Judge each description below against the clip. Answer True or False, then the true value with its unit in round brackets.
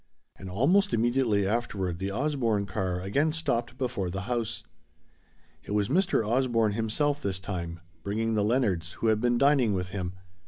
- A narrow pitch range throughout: False (4.8 semitones)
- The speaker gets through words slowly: False (160 wpm)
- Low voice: True (110 Hz)